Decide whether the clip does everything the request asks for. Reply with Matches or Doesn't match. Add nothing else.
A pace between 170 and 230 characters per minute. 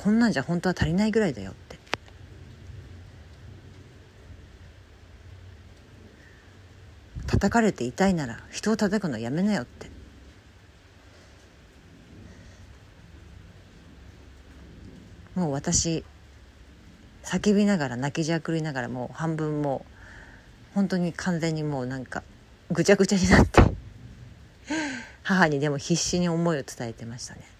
Matches